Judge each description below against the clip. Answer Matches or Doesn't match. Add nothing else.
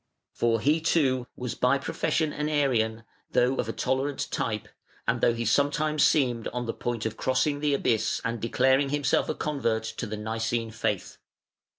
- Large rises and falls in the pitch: Doesn't match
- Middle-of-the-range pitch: Doesn't match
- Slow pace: Doesn't match